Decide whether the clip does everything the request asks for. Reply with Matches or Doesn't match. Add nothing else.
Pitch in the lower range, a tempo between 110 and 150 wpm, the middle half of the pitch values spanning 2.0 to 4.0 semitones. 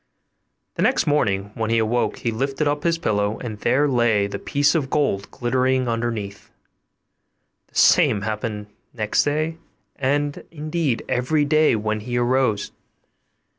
Doesn't match